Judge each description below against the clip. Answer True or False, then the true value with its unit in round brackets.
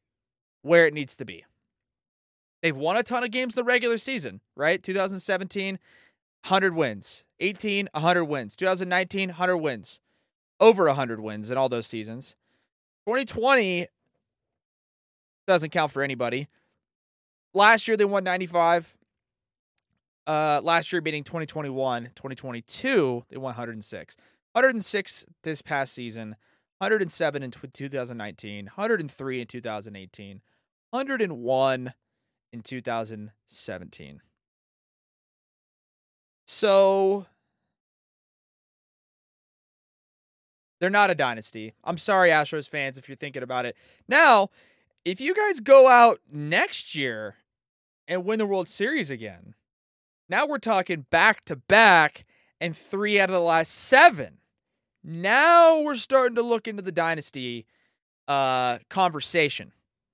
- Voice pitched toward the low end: False (160 Hz)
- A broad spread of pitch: True (7.7 semitones)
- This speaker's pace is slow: True (115 wpm)